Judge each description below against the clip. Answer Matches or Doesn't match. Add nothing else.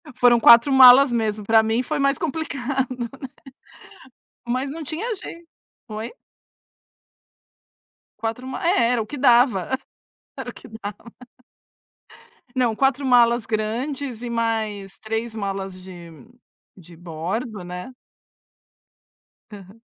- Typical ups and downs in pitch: Matches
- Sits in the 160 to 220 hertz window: Doesn't match